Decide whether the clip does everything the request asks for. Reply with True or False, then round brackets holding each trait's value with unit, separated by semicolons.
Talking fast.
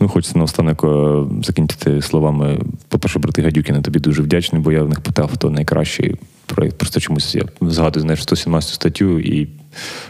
True (170 wpm)